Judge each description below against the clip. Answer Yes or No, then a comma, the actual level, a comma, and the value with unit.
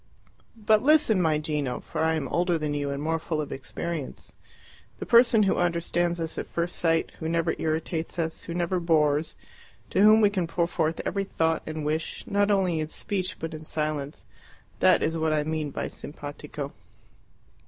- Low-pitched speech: No, medium, 165 Hz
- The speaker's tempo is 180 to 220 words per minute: Yes, average, 185 wpm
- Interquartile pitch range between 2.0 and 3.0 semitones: Yes, narrow, 2.4 semitones